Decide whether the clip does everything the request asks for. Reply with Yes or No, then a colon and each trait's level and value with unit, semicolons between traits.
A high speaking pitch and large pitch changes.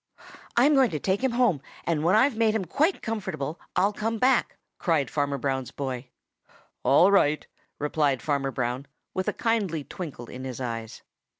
No: medium, 160 Hz; wide, 8.2 semitones